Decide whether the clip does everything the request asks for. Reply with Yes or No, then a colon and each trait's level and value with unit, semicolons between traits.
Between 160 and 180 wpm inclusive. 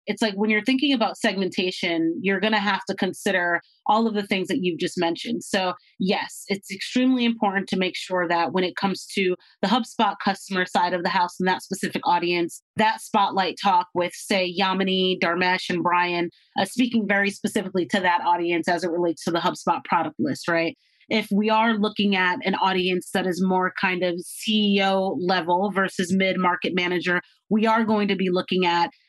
No: average, 195 wpm